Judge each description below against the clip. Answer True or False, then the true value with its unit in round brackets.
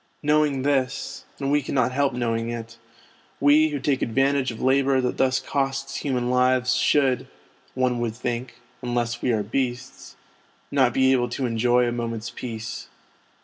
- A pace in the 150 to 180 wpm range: True (155 wpm)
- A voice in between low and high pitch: False (130 Hz)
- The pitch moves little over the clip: True (2.2 semitones)